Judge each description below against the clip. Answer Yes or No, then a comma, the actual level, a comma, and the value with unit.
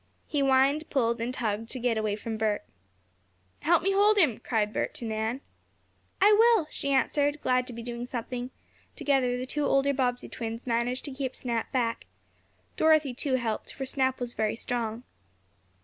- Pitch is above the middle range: Yes, very high, 250 Hz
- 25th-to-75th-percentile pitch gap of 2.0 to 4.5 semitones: Yes, average, 3.3 semitones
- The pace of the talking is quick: No, average, 175 wpm